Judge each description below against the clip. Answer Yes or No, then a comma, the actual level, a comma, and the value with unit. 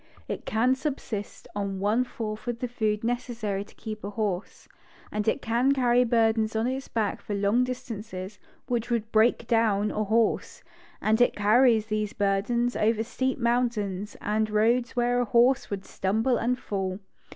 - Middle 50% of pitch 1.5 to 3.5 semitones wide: Yes, narrow, 2.6 semitones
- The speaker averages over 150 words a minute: Yes, average, 160 wpm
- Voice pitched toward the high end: Yes, high, 225 Hz